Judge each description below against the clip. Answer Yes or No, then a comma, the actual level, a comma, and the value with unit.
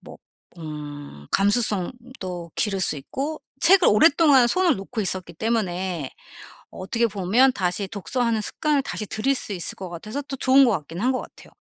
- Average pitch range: No, wide, 6.3 semitones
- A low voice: No, high, 210 Hz